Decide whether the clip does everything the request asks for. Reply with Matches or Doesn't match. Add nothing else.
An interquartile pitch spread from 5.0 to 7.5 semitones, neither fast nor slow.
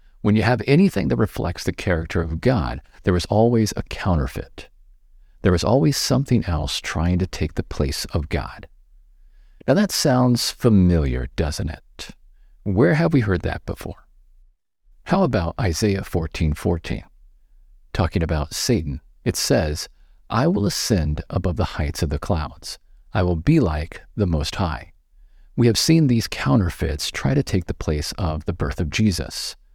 Matches